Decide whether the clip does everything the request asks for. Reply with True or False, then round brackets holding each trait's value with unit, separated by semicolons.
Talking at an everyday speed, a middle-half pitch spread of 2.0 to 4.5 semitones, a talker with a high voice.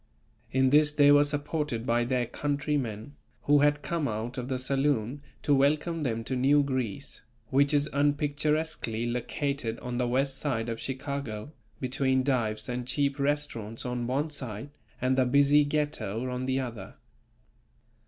False (155 wpm; 3.1 semitones; 135 Hz)